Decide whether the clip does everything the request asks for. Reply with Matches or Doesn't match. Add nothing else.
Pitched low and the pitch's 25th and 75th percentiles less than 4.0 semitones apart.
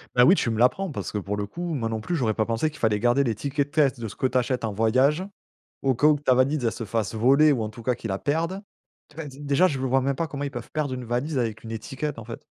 Doesn't match